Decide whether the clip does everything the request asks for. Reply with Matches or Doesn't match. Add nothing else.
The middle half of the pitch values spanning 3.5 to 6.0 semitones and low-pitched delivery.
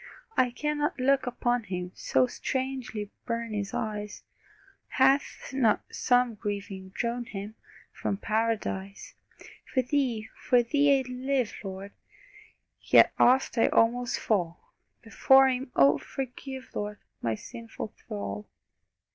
Doesn't match